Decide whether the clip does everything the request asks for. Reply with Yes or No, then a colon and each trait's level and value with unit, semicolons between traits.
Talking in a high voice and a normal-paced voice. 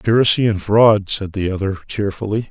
No: low, 100 Hz; average, 165 wpm